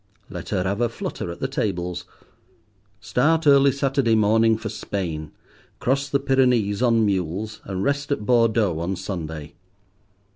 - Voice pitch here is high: No, low, 110 Hz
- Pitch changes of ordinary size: No, wide, 5.9 semitones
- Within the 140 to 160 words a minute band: Yes, average, 145 wpm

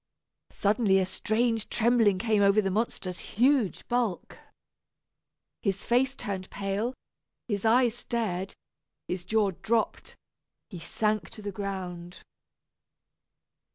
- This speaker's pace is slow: Yes, slow, 110 wpm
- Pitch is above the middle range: Yes, high, 210 Hz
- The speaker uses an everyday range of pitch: Yes, average, 3.3 semitones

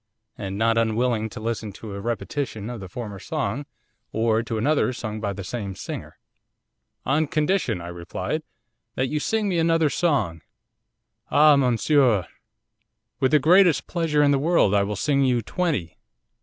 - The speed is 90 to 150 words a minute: No, average, 160 wpm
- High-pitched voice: No, low, 120 Hz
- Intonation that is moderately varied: No, wide, 6.0 semitones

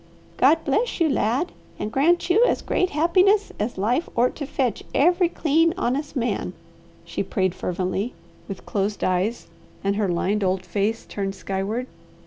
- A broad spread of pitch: Yes, wide, 8.5 semitones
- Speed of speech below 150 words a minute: No, average, 155 wpm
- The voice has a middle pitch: No, high, 240 Hz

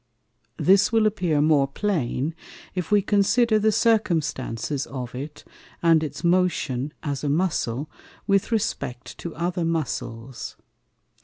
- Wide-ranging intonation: Yes, wide, 6.2 semitones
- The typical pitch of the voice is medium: Yes, medium, 165 Hz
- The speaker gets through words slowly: Yes, slow, 125 wpm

